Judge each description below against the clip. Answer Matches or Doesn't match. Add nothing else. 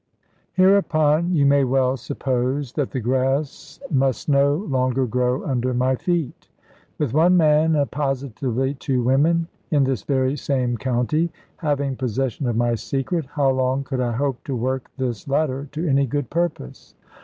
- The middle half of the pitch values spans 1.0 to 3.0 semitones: Matches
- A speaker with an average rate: Matches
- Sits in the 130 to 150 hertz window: Matches